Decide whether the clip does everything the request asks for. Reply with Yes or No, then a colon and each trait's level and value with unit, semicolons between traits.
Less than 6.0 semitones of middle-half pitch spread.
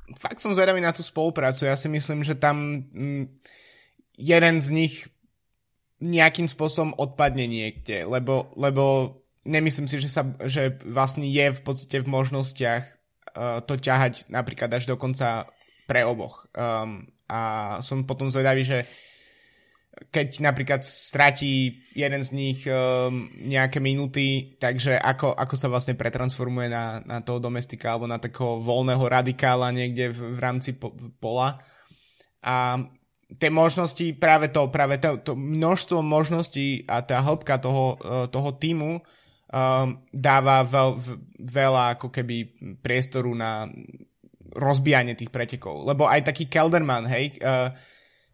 Yes: average, 2.7 semitones